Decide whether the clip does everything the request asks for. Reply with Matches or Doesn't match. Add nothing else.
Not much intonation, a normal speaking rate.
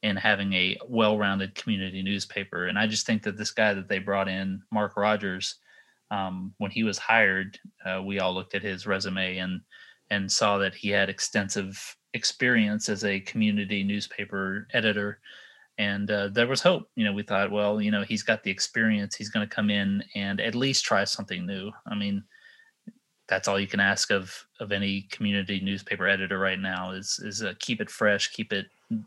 Matches